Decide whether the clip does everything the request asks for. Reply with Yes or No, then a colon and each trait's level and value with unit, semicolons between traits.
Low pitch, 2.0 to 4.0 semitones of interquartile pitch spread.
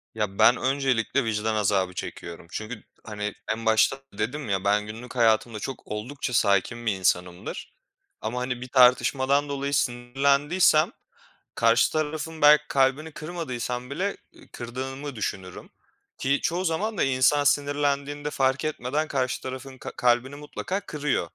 No: low, 130 Hz; average, 4.5 semitones